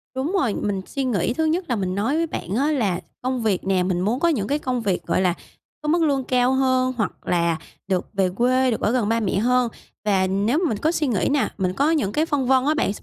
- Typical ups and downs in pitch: No, wide, 5.7 semitones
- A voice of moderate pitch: No, high, 245 Hz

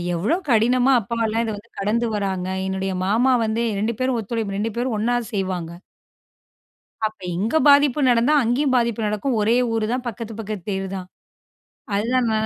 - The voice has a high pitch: Yes, high, 225 Hz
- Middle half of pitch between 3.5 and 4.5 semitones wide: No, average, 2.8 semitones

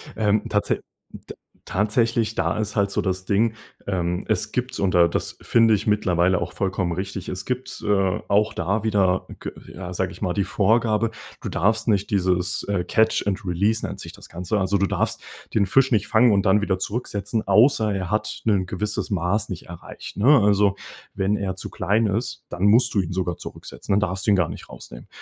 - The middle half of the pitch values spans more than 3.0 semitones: No, narrow, 2.6 semitones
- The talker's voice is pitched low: Yes, low, 100 Hz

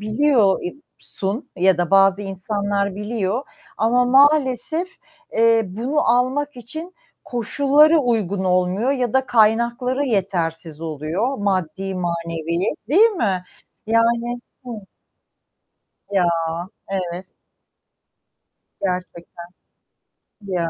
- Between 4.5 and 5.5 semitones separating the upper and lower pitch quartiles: Yes, average, 5.1 semitones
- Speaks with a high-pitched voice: Yes, high, 210 Hz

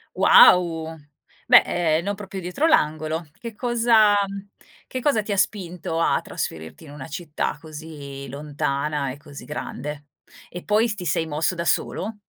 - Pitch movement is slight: No, wide, 5.5 semitones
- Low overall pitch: No, medium, 165 Hz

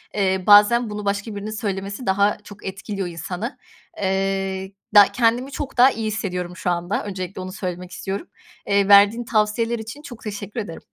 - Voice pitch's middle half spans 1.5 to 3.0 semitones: Yes, narrow, 2.5 semitones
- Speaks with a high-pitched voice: Yes, high, 205 Hz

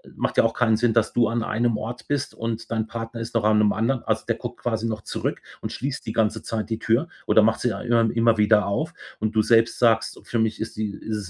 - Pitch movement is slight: Yes, narrow, 1.3 semitones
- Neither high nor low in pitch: No, low, 115 Hz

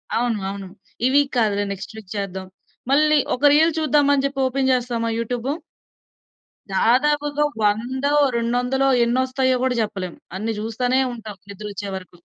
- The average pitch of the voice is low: No, high, 245 Hz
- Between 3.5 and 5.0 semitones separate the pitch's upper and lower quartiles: Yes, average, 4.4 semitones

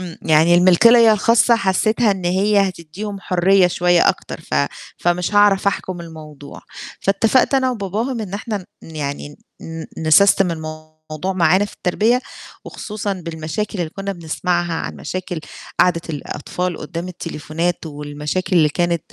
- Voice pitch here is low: No, medium, 180 Hz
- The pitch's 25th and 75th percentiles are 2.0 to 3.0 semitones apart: No, average, 3.6 semitones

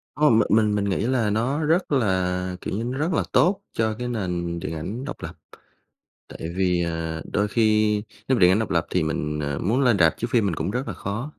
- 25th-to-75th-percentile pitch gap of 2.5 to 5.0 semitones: No, wide, 5.4 semitones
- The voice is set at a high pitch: No, low, 105 Hz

